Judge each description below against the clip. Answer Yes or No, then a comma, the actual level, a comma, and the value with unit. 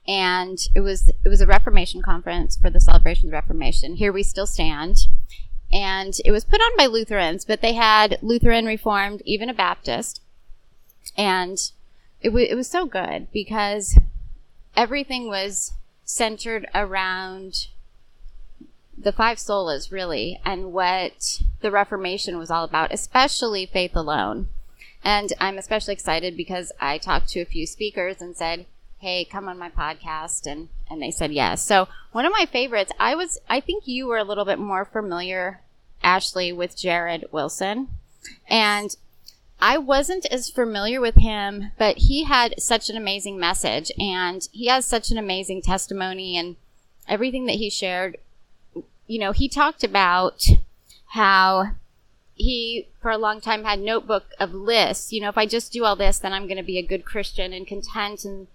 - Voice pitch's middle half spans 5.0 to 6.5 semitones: No, average, 3.3 semitones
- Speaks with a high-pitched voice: Yes, high, 200 Hz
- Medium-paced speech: Yes, average, 165 wpm